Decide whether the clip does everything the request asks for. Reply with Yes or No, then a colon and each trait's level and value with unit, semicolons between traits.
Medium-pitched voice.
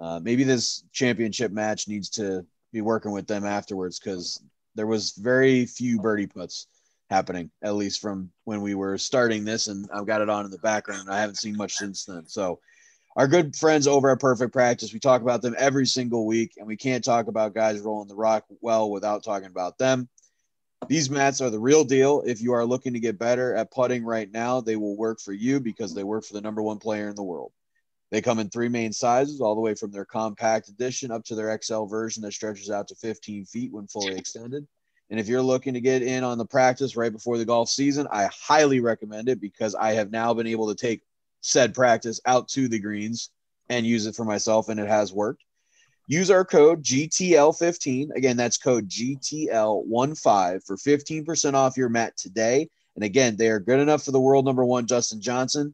No: low, 115 Hz